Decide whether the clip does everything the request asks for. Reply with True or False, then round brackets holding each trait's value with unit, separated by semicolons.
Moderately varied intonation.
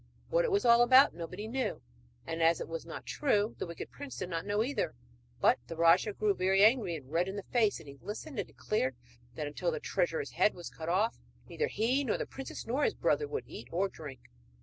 False (7.6 semitones)